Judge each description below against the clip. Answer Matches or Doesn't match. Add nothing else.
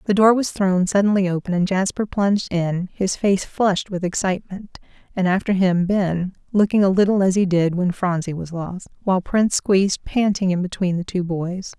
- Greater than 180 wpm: Matches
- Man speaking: Doesn't match